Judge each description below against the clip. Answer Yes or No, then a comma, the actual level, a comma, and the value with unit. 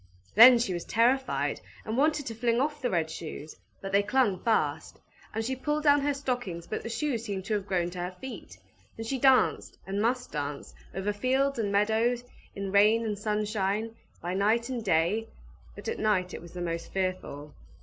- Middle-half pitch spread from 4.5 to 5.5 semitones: Yes, average, 4.8 semitones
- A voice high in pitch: Yes, high, 215 Hz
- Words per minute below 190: No, average, 195 wpm